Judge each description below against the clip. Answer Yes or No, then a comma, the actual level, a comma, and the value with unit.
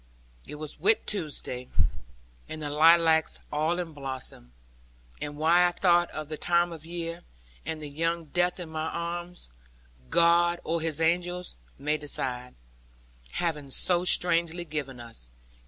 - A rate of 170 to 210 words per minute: No, average, 140 wpm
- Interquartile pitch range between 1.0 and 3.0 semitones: Yes, narrow, 2.6 semitones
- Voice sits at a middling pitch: Yes, medium, 165 Hz